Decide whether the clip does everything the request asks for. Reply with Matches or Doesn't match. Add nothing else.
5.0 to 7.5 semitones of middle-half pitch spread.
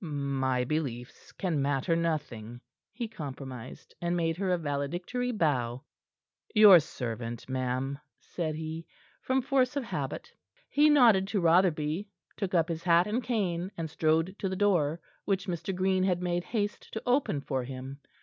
Matches